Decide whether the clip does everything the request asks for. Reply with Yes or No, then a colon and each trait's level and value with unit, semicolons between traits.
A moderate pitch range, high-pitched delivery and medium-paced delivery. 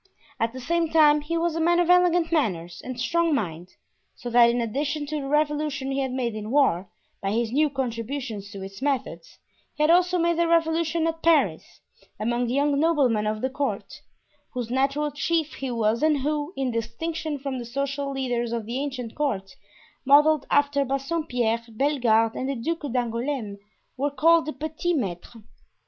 Yes: average, 4.7 semitones; very high, 275 Hz; average, 180 wpm